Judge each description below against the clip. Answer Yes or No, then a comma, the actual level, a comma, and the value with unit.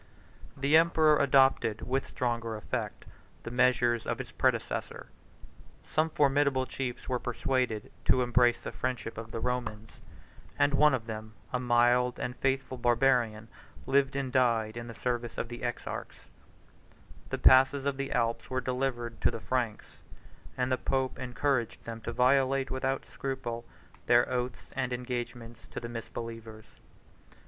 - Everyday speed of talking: Yes, average, 145 wpm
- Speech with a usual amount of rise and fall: No, narrow, 2.2 semitones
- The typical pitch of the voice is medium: No, low, 125 Hz